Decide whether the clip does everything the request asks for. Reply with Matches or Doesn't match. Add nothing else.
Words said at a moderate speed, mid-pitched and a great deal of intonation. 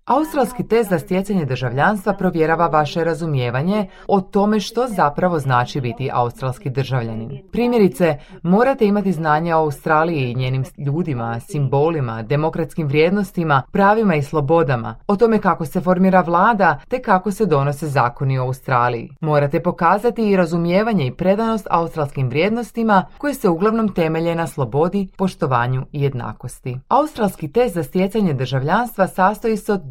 Matches